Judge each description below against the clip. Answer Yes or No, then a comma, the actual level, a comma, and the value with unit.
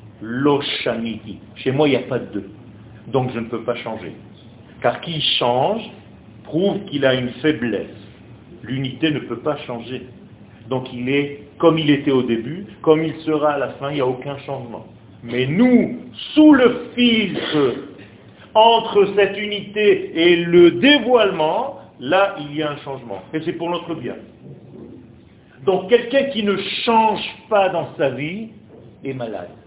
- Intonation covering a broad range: Yes, wide, 8.5 semitones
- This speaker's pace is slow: No, average, 160 wpm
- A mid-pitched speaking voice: Yes, medium, 145 Hz